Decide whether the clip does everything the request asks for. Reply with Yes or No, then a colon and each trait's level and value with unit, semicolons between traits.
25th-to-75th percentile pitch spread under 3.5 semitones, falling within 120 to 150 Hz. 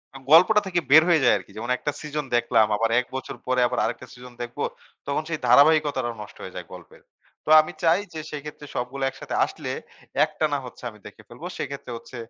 No: average, 4.0 semitones; medium, 140 Hz